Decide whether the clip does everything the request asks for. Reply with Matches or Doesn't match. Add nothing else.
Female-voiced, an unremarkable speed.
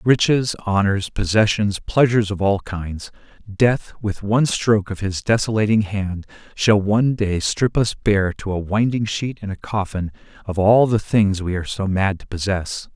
Doesn't match